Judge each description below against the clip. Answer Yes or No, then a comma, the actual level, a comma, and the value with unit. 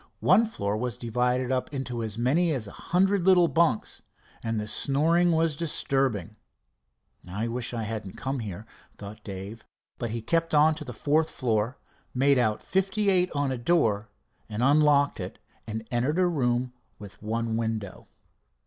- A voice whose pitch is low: Yes, low, 125 Hz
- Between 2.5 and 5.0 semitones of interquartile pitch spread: No, wide, 5.6 semitones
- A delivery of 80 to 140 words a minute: No, average, 160 wpm